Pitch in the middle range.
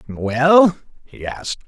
Yes: medium, 145 Hz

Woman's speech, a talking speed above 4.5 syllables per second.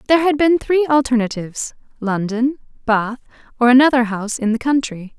Yes: female; 5.7 syllables/s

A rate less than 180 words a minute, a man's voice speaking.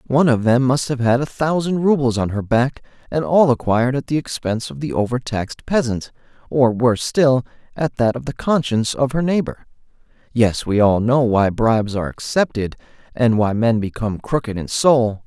No: average, 190 wpm; male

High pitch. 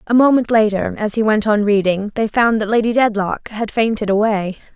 Yes: high, 215 Hz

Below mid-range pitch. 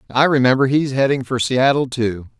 Yes: low, 130 Hz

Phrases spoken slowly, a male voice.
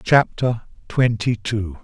Yes: slow, 100 wpm; male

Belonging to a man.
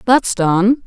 No: female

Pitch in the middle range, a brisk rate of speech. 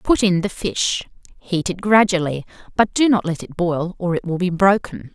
Yes: medium, 180 Hz; fast, 210 wpm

